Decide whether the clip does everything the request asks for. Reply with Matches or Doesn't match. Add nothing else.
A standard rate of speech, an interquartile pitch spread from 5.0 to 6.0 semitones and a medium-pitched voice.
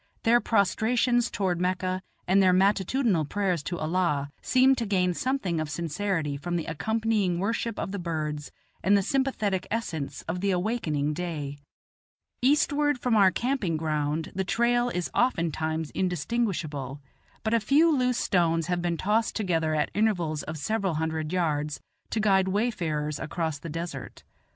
Matches